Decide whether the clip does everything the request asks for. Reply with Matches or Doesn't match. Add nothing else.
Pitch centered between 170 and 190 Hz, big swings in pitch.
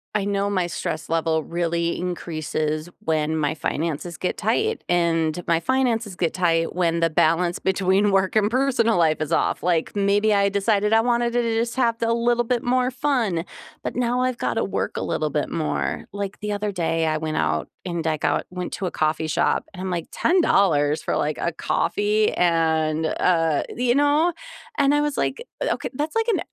Matches